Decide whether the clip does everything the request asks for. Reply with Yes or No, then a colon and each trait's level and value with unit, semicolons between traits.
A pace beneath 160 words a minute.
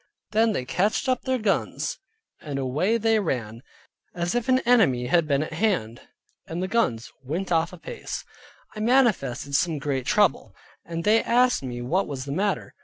No: average, 175 wpm